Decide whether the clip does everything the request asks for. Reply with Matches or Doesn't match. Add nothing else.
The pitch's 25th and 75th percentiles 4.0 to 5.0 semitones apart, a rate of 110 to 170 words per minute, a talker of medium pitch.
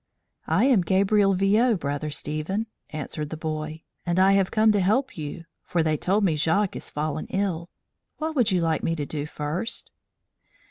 Doesn't match